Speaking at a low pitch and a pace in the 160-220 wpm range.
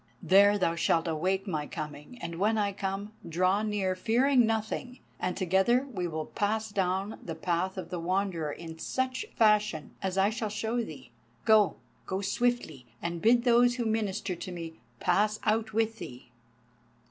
No: high, 195 Hz; average, 165 wpm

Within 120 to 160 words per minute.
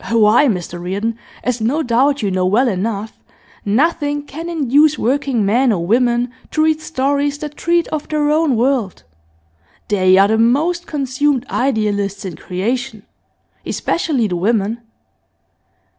Yes: average, 140 wpm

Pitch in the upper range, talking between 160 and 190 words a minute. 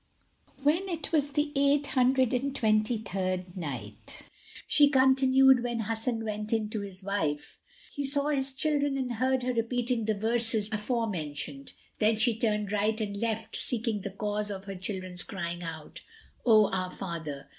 Yes: high, 220 Hz; average, 165 wpm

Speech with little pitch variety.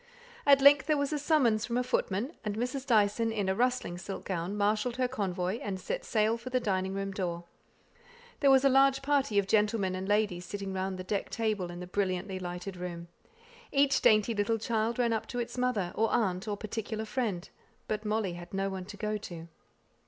No: average, 4.3 semitones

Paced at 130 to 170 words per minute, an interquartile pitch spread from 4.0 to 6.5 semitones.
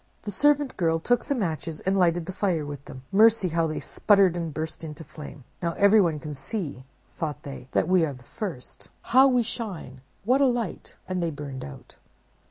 No: average, 195 wpm; wide, 5.5 semitones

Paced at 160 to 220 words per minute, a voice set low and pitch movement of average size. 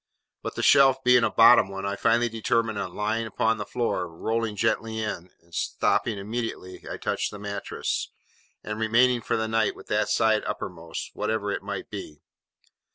No: average, 170 wpm; low, 110 Hz; narrow, 2.3 semitones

